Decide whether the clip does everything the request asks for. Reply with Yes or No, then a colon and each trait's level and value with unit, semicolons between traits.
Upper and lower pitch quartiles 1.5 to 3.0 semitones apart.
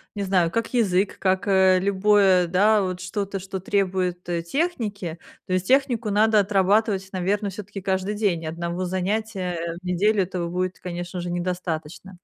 Yes: narrow, 2.4 semitones